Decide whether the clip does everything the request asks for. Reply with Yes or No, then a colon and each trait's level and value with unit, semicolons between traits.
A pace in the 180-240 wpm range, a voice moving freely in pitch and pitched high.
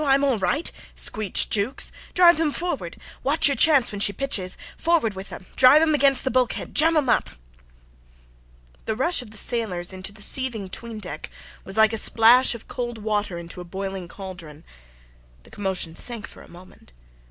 Yes: average, 185 wpm; wide, 6.0 semitones; high, 220 Hz